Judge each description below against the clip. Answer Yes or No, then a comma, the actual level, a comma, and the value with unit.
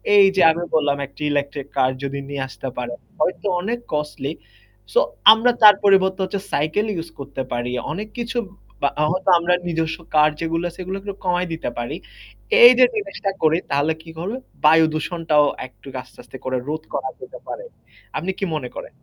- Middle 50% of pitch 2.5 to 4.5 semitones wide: No, average, 5.0 semitones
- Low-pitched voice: No, medium, 160 Hz